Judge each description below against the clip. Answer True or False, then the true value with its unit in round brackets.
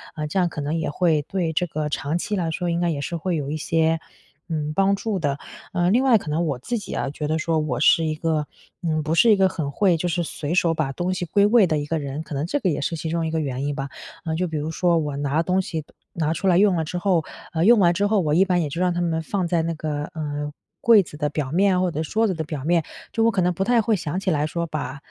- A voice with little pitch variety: False (3.2 semitones)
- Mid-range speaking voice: True (165 Hz)